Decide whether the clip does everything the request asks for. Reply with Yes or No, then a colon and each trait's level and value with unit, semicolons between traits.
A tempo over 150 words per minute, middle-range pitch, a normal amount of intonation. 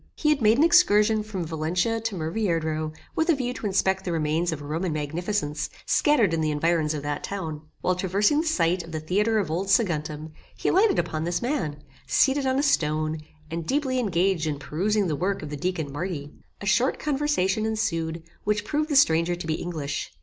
No: average, 200 wpm; medium, 180 Hz; wide, 5.9 semitones